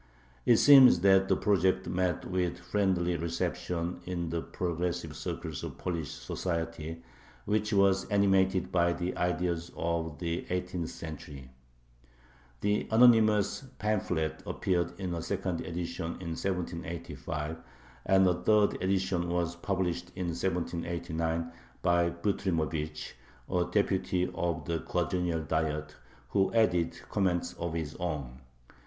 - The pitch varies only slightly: Yes, narrow, 2.2 semitones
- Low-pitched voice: Yes, very low, 85 Hz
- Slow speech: Yes, slow, 125 wpm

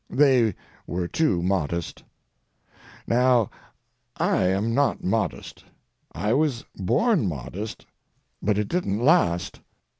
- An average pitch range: No, wide, 6.2 semitones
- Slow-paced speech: Yes, slow, 100 wpm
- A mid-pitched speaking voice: No, low, 105 Hz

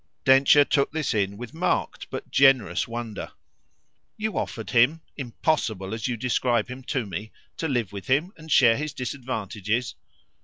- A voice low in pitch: Yes, low, 125 Hz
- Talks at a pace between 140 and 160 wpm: Yes, average, 155 wpm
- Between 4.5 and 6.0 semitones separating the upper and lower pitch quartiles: No, average, 4.1 semitones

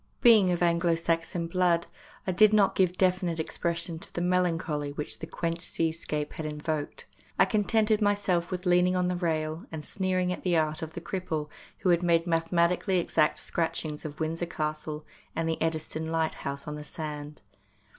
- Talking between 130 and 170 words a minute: No, average, 180 wpm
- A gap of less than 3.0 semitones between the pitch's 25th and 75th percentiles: Yes, narrow, 2.4 semitones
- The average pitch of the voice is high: No, medium, 170 Hz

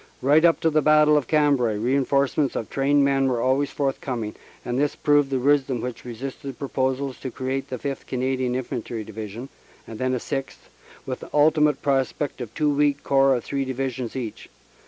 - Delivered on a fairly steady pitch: Yes, narrow, 2.2 semitones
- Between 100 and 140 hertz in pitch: Yes, low, 135 Hz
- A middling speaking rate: Yes, average, 185 wpm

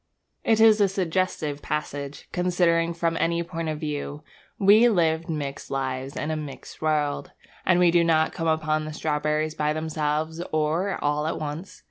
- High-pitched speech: No, medium, 160 Hz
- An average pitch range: No, narrow, 2.2 semitones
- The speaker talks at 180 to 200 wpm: No, average, 165 wpm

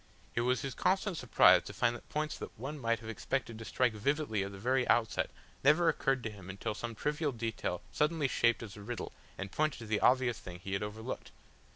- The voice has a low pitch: Yes, low, 120 Hz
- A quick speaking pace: Yes, fast, 220 wpm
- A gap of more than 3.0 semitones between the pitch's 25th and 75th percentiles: Yes, average, 4.4 semitones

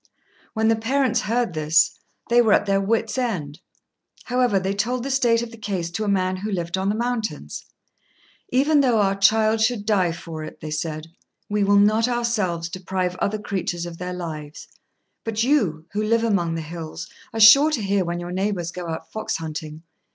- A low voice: No, high, 200 Hz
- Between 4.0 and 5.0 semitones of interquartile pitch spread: Yes, average, 4.7 semitones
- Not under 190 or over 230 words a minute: Yes, average, 195 wpm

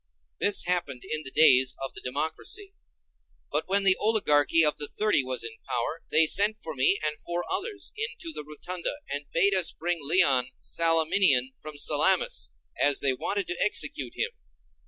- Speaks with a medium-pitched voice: Yes, medium, 160 Hz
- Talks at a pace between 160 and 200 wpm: Yes, average, 175 wpm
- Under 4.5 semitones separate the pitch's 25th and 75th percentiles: No, wide, 5.5 semitones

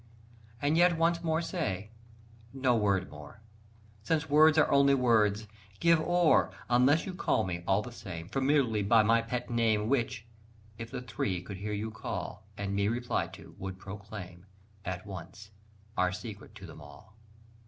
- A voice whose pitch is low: Yes, low, 110 Hz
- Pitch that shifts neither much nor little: No, wide, 5.9 semitones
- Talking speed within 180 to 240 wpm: No, average, 165 wpm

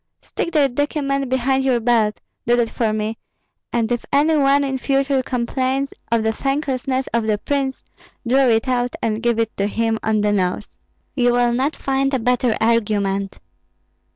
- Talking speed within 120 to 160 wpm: No, average, 175 wpm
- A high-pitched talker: Yes, high, 245 Hz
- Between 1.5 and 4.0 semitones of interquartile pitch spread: Yes, average, 3.4 semitones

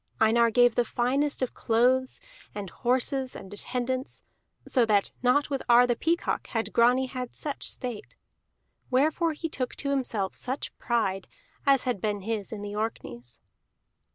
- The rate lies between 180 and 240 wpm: No, average, 155 wpm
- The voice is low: No, high, 245 Hz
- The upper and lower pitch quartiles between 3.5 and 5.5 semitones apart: No, average, 3.0 semitones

